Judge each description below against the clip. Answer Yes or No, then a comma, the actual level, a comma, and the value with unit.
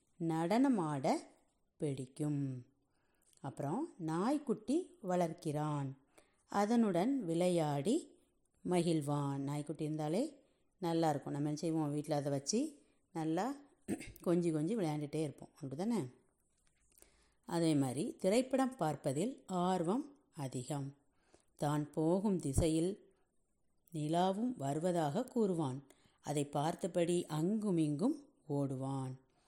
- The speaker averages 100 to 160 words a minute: No, average, 80 wpm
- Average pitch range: No, wide, 6.2 semitones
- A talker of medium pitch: Yes, medium, 165 Hz